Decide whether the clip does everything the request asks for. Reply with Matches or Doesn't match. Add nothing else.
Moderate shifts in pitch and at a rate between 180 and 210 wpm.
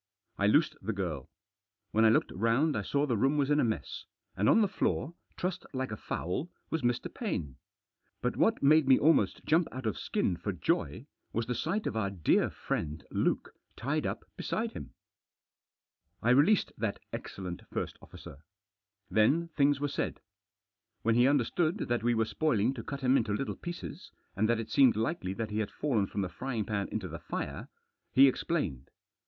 Doesn't match